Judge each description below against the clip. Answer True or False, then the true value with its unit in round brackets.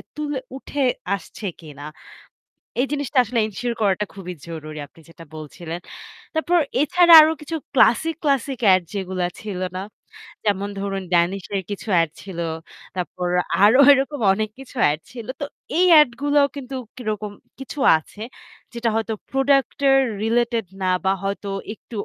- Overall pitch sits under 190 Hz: False (220 Hz)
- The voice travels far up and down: True (6.3 semitones)